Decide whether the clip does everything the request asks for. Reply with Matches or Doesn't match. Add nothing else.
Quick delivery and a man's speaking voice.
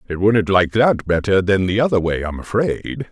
Matches